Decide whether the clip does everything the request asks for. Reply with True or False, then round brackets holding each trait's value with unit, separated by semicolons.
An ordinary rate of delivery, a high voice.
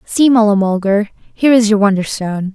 True (165 wpm; 210 Hz)